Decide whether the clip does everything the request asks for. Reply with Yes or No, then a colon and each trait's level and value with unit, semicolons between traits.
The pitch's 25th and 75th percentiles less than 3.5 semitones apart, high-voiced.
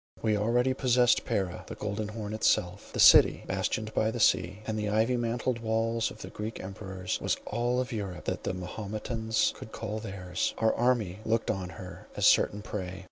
No: average, 2.9 semitones; low, 110 Hz